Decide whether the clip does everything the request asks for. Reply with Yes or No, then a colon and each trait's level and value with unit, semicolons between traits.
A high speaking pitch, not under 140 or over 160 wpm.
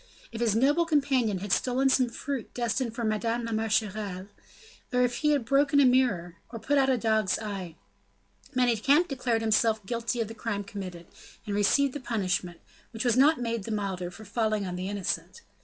No: high, 225 Hz; average, 185 wpm